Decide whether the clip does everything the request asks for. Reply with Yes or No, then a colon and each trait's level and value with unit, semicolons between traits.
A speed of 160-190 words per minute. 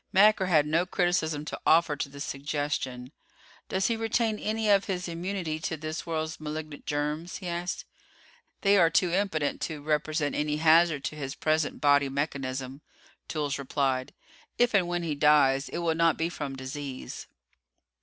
Yes: average, 165 wpm